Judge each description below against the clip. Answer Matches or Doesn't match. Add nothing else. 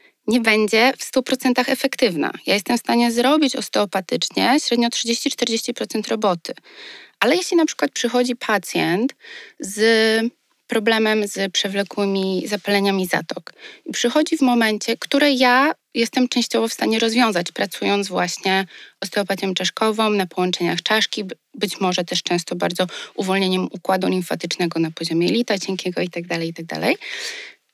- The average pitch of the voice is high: Matches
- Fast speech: Doesn't match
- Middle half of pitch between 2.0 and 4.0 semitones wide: Doesn't match